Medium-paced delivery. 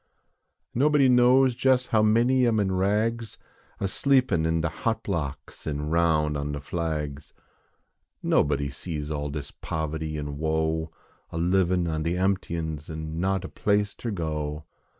Yes: average, 150 wpm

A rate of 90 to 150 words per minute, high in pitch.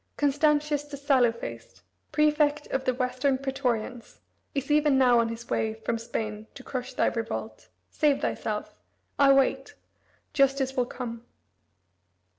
Yes: slow, 135 wpm; very high, 265 Hz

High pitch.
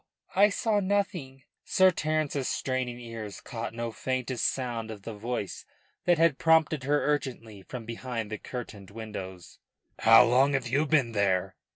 No: low, 125 Hz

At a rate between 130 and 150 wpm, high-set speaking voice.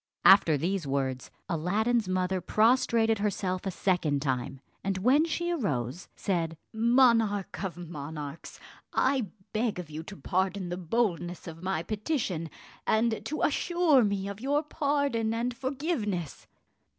Yes: slow, 135 wpm; high, 200 Hz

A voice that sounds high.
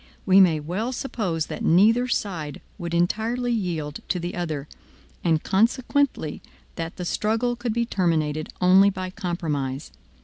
No: medium, 180 Hz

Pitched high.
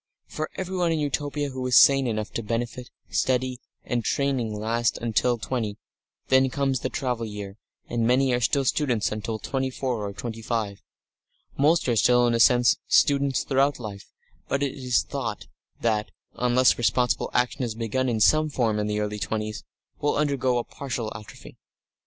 No: low, 125 Hz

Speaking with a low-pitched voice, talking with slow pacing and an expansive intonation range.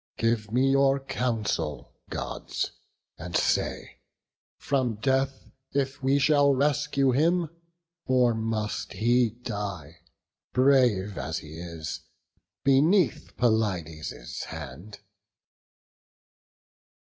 Yes: low, 120 Hz; slow, 85 wpm; wide, 5.8 semitones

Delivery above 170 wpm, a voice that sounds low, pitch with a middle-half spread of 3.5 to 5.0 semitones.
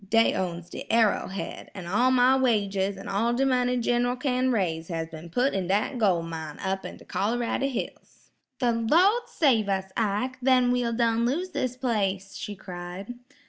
No: average, 180 wpm; high, 225 Hz; average, 4.6 semitones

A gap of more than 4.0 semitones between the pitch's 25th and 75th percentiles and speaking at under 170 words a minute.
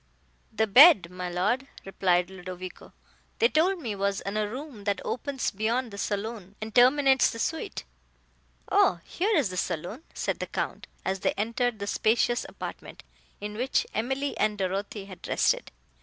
Yes: average, 4.7 semitones; average, 160 wpm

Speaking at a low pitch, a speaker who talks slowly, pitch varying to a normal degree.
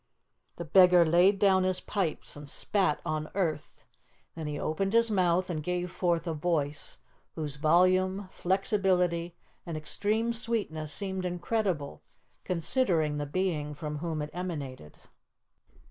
No: medium, 175 Hz; slow, 130 wpm; average, 3.6 semitones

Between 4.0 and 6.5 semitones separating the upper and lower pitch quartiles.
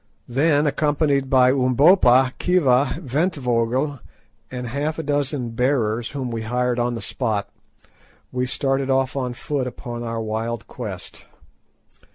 No: average, 3.0 semitones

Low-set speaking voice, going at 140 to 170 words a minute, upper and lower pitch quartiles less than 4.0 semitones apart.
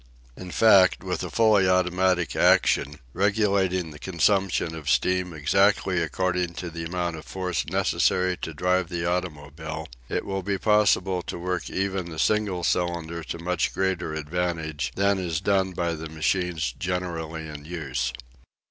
Yes: very low, 90 Hz; average, 150 wpm; narrow, 2.5 semitones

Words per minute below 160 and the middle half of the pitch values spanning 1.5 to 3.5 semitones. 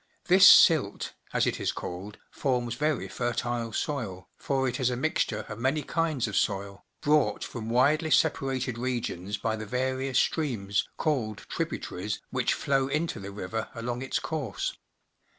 No: average, 150 wpm; average, 4.3 semitones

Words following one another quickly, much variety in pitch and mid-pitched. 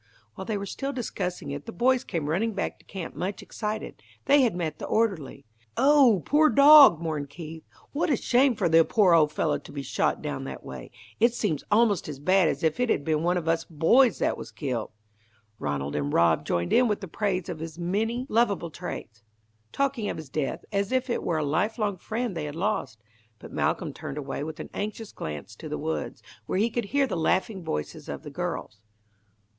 Yes: fast, 210 wpm; wide, 6.8 semitones; medium, 180 Hz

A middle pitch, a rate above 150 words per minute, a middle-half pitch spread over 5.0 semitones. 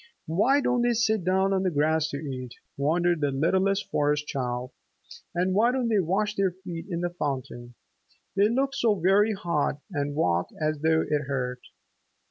Yes: medium, 170 Hz; average, 175 wpm; wide, 5.4 semitones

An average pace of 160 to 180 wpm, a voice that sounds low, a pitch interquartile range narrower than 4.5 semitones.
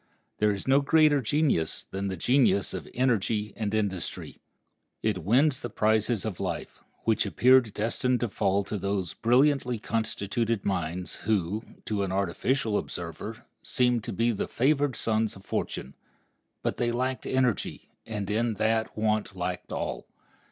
No: average, 150 wpm; low, 110 Hz; average, 3.8 semitones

